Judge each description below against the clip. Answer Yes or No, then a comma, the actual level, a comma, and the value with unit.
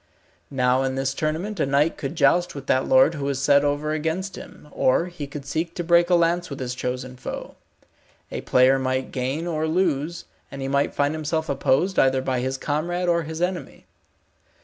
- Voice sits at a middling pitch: Yes, medium, 145 Hz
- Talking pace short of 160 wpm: No, average, 195 wpm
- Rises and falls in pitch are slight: No, average, 4.0 semitones